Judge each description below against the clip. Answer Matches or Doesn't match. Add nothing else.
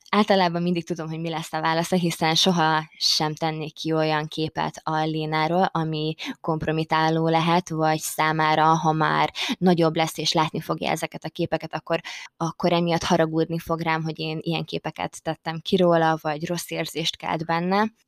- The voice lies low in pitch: Doesn't match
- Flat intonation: Matches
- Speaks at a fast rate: Matches